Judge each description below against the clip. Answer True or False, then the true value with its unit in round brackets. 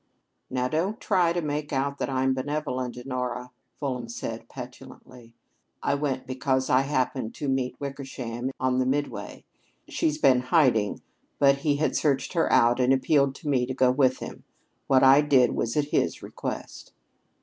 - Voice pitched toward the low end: True (130 Hz)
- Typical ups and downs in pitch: False (2.2 semitones)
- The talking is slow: False (165 wpm)